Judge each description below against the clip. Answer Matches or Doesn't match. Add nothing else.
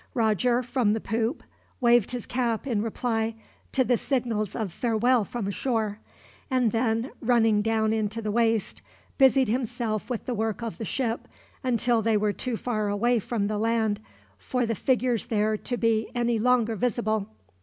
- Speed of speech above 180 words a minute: Doesn't match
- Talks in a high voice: Matches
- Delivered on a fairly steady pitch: Matches